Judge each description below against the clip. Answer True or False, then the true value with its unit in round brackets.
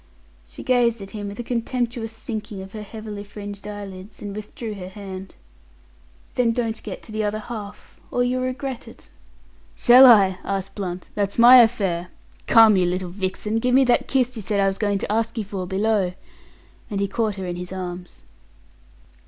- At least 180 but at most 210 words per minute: True (185 wpm)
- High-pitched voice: True (210 Hz)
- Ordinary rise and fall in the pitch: True (3.2 semitones)